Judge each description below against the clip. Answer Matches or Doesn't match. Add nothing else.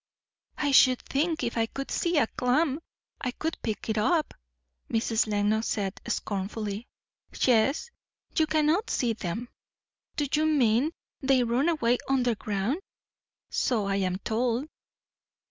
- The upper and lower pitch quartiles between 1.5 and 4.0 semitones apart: Doesn't match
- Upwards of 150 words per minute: Doesn't match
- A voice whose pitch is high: Matches